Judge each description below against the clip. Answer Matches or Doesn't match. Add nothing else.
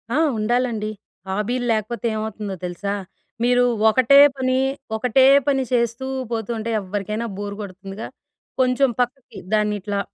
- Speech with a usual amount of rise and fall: Matches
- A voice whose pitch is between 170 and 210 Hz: Doesn't match